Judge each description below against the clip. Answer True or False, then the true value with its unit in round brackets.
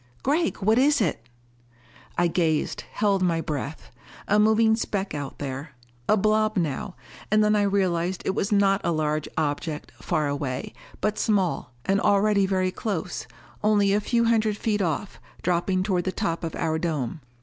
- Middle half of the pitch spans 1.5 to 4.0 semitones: False (4.8 semitones)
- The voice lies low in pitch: False (190 Hz)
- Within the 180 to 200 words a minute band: False (165 wpm)